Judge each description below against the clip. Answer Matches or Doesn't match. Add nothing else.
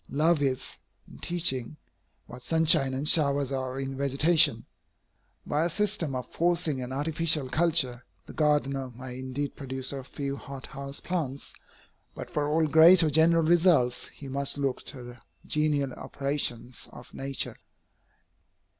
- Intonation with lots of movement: Doesn't match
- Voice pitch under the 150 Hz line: Matches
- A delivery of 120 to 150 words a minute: Matches